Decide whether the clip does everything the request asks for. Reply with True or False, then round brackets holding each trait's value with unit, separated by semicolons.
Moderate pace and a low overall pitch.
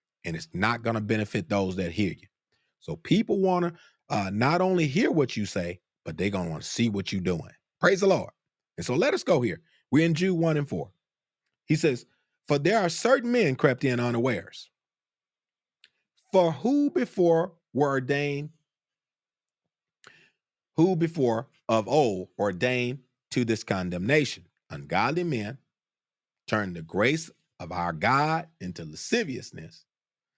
True (155 wpm; 130 Hz)